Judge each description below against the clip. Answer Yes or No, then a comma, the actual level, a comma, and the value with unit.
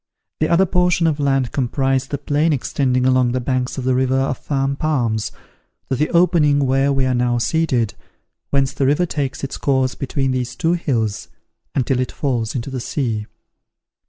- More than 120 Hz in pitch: Yes, low, 135 Hz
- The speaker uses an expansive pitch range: No, narrow, 2.4 semitones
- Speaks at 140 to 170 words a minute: No, average, 180 wpm